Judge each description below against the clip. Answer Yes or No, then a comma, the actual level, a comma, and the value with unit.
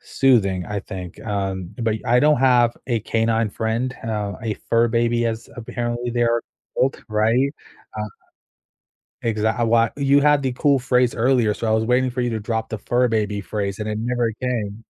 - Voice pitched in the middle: No, low, 115 Hz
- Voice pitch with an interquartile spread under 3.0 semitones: Yes, narrow, 2.4 semitones